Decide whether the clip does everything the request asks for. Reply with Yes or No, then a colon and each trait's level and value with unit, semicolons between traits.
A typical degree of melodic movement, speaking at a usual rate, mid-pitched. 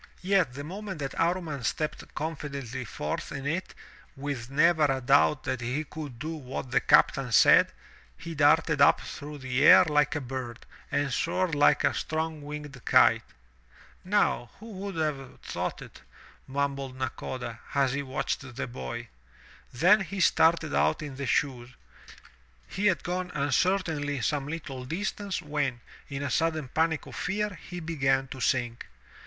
Yes: average, 3.8 semitones; average, 155 wpm; medium, 145 Hz